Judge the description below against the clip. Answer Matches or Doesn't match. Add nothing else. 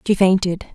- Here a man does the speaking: Doesn't match